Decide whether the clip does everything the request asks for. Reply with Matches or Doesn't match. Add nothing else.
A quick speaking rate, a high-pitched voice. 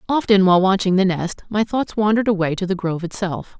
Matches